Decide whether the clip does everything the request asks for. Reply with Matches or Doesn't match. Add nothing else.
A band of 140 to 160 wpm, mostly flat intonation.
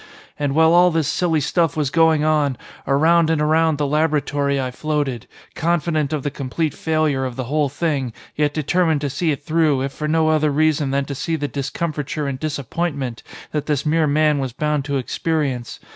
Doesn't match